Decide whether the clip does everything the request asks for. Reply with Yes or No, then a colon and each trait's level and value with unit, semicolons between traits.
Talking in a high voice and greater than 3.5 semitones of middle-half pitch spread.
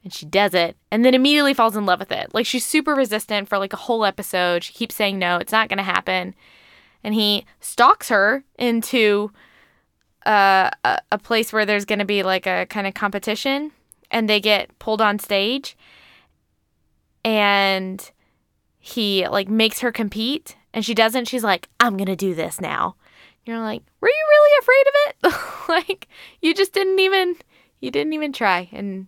Yes: high, 215 Hz; average, 4.6 semitones